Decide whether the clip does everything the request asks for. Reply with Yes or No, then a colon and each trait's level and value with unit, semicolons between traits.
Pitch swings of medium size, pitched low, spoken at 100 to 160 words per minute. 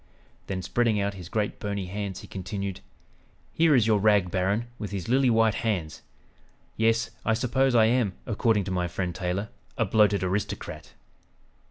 No: average, 3.0 semitones; low, 105 Hz; average, 170 wpm